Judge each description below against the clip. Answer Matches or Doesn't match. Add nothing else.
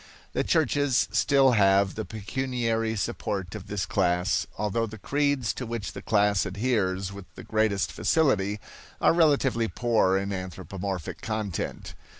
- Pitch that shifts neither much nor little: Matches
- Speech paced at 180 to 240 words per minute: Doesn't match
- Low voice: Matches